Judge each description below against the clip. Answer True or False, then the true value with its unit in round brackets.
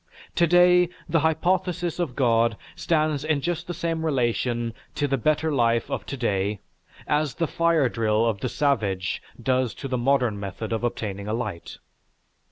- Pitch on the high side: False (135 Hz)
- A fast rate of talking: False (170 wpm)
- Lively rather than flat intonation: True (5.8 semitones)